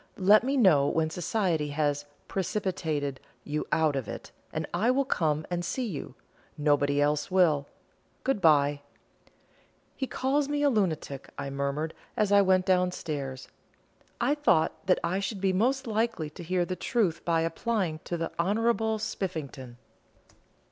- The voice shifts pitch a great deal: Yes, wide, 6.1 semitones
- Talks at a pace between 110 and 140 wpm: No, average, 155 wpm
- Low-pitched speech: No, medium, 175 Hz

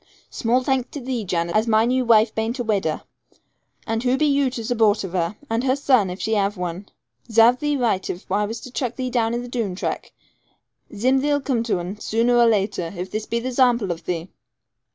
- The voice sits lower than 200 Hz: No, high, 225 Hz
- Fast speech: Yes, fast, 225 wpm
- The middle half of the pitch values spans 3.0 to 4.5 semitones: Yes, average, 3.8 semitones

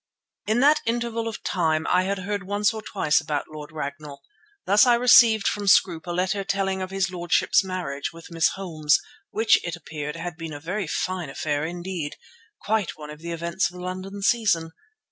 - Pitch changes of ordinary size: Yes, average, 4.0 semitones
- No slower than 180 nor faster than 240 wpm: Yes, average, 190 wpm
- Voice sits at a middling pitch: Yes, medium, 180 Hz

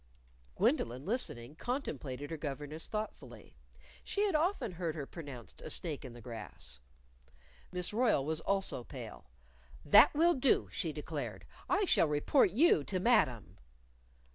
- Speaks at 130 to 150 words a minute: Yes, average, 140 wpm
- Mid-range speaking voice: Yes, medium, 165 Hz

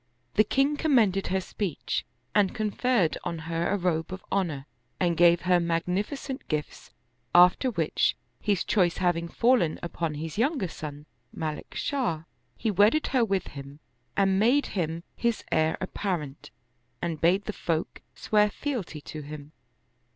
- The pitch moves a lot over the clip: No, average, 4.7 semitones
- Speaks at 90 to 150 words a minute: Yes, average, 145 wpm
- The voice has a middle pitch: Yes, medium, 180 Hz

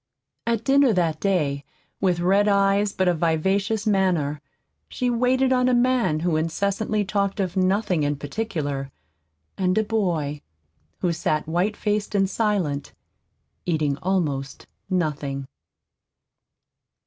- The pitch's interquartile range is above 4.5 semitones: Yes, average, 5.1 semitones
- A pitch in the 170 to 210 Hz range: Yes, medium, 185 Hz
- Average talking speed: No, slow, 125 wpm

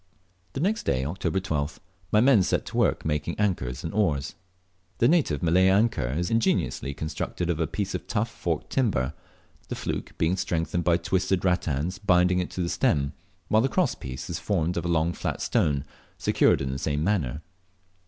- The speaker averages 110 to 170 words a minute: No, average, 185 wpm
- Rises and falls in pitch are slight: No, average, 4.6 semitones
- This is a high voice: No, very low, 85 Hz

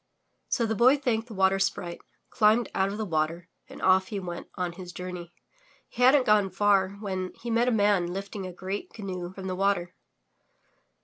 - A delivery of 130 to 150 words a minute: No, average, 190 wpm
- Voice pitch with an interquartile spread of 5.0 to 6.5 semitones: No, average, 2.7 semitones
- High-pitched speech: Yes, high, 195 Hz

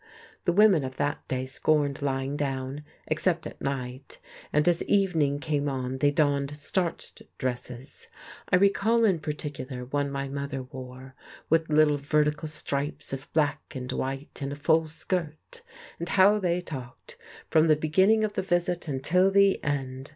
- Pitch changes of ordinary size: Yes, average, 3.9 semitones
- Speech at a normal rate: Yes, average, 160 wpm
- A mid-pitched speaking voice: Yes, medium, 145 Hz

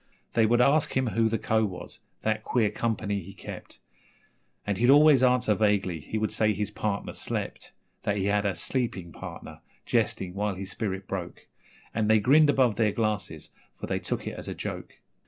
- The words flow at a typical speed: Yes, average, 190 wpm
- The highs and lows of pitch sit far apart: No, average, 3.0 semitones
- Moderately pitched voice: No, low, 110 Hz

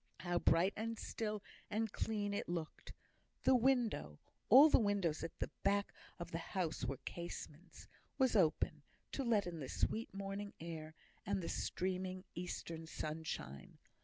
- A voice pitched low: No, medium, 185 Hz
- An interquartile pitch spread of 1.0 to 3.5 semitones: No, average, 4.2 semitones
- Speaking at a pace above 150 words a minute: No, average, 145 wpm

